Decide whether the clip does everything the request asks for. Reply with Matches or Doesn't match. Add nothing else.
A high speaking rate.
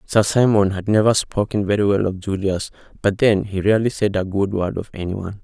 Matches